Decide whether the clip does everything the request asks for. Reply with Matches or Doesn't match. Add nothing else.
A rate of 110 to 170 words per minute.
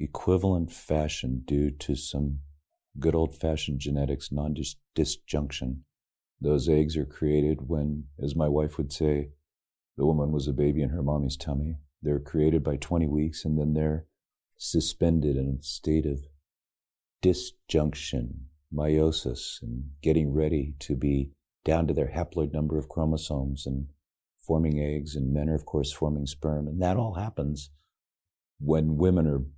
Matches